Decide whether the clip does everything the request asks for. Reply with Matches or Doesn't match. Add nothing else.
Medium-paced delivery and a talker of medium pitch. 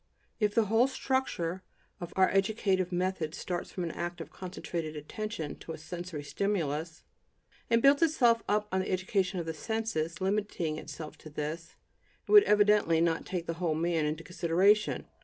Matches